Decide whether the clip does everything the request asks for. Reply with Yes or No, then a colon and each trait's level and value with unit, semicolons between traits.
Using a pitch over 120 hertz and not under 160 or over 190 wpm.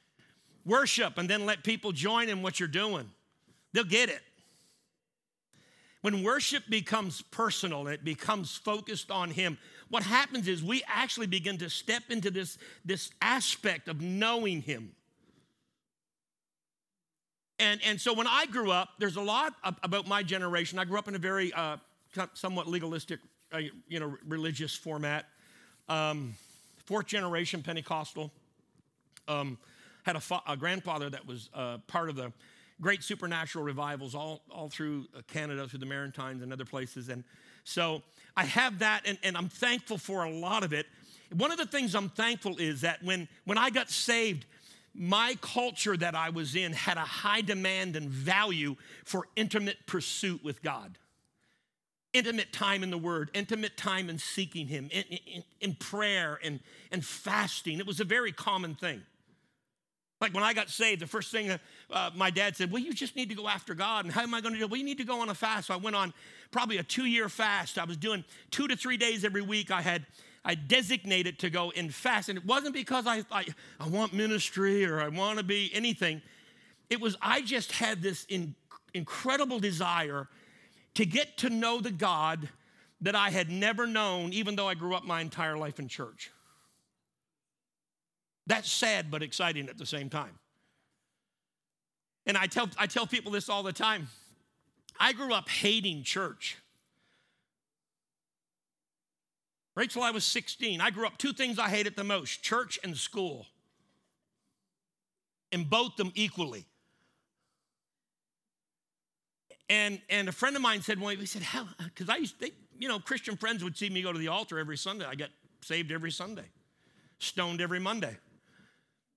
Yes: high, 190 Hz; average, 175 wpm